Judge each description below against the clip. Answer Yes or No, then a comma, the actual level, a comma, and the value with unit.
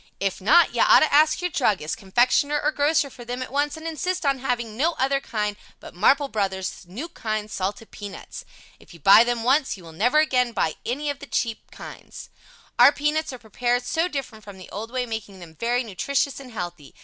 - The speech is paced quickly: Yes, fast, 215 wpm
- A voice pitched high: Yes, high, 245 Hz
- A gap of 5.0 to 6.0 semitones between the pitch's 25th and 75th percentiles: Yes, wide, 5.5 semitones